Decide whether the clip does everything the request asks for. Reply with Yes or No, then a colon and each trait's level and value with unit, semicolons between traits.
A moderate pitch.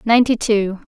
No: high, 220 Hz